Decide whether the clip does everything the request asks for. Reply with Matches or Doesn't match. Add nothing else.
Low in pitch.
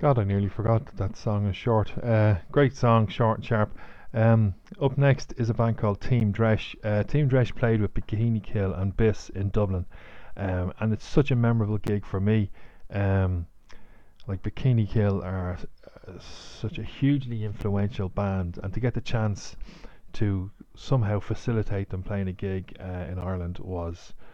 Matches